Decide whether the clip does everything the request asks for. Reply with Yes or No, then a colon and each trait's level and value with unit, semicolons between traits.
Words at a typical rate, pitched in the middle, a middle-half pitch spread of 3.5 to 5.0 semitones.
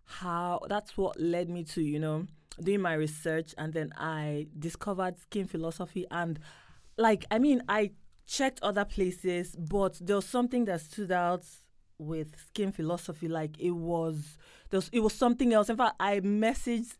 Yes: average, 170 wpm; medium, 180 Hz; average, 4.0 semitones